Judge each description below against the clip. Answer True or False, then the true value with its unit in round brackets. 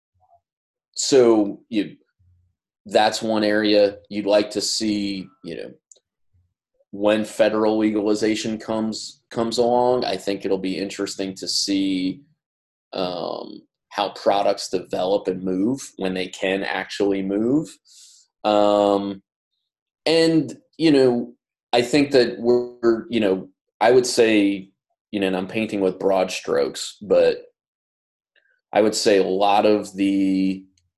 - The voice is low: True (105 Hz)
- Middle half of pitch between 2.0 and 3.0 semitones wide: False (3.7 semitones)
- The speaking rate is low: True (125 wpm)